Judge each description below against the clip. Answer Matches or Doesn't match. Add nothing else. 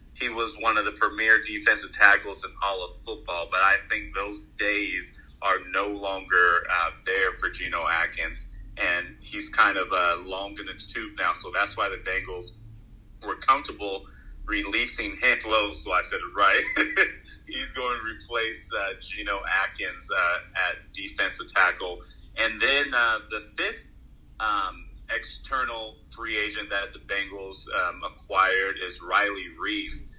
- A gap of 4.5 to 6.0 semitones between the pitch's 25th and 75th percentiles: Doesn't match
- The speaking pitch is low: Matches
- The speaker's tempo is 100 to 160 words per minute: Matches